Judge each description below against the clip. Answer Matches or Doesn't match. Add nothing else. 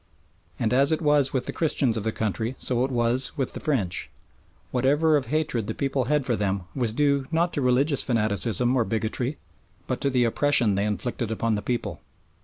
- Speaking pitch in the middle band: Doesn't match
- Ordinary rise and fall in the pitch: Matches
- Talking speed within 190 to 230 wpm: Matches